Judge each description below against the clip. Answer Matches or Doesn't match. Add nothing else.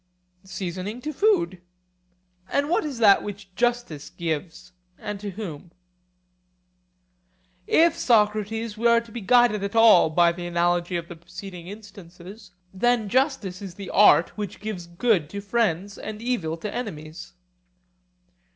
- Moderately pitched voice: Doesn't match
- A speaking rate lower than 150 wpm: Matches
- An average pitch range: Matches